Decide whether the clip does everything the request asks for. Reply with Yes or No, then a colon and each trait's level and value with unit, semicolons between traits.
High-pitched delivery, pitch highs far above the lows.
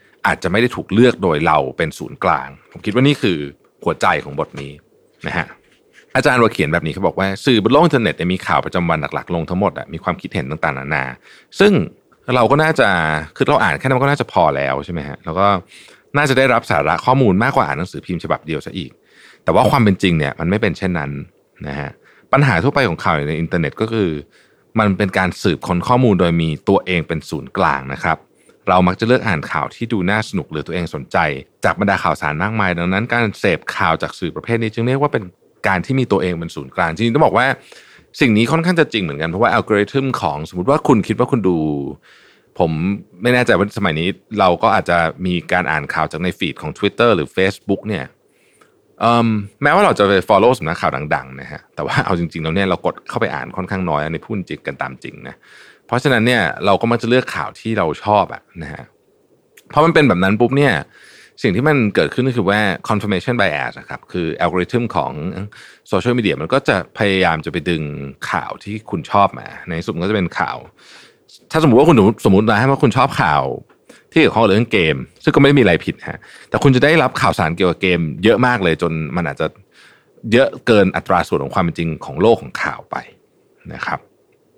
No: very low, 95 Hz; wide, 5.9 semitones